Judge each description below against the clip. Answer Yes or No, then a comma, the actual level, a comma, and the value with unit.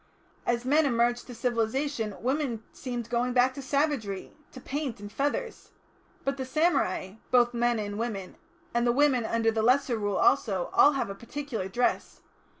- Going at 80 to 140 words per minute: No, average, 165 wpm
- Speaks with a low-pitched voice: No, high, 240 Hz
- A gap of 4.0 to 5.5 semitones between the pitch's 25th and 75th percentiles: No, average, 3.6 semitones